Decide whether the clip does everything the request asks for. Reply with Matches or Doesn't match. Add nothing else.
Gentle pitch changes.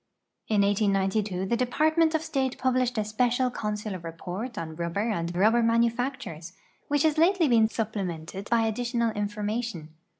Doesn't match